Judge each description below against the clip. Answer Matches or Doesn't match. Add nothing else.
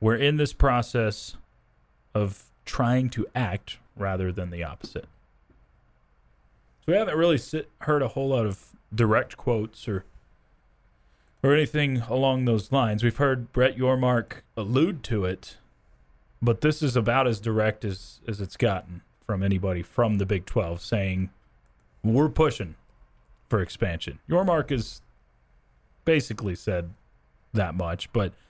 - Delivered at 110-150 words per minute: Matches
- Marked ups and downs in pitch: Matches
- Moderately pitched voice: Doesn't match